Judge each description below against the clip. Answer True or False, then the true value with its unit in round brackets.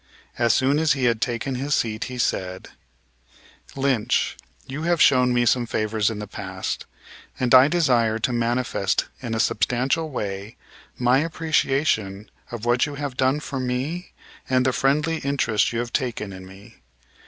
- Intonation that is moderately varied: True (3.7 semitones)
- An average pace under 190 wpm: True (165 wpm)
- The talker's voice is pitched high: False (125 Hz)